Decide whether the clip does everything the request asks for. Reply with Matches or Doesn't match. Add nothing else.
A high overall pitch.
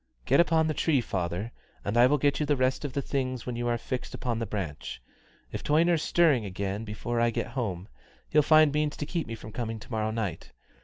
Doesn't match